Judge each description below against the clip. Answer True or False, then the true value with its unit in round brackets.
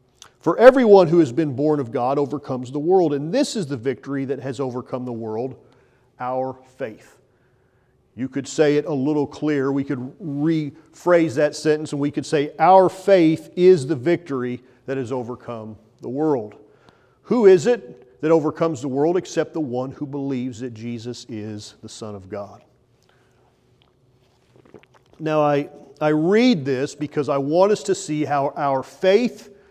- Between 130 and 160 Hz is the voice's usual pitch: True (140 Hz)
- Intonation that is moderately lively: True (4.0 semitones)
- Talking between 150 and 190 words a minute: True (165 wpm)